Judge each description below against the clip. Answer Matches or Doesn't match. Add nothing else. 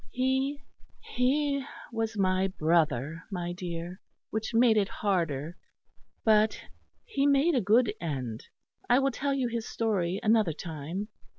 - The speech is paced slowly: Matches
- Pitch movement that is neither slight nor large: Doesn't match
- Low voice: Doesn't match